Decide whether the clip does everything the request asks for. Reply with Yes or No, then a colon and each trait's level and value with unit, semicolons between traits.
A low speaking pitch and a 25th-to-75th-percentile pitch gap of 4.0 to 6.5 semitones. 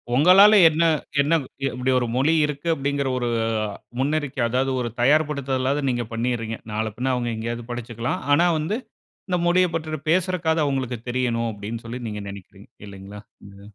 Yes: low, 130 Hz; average, 4.8 semitones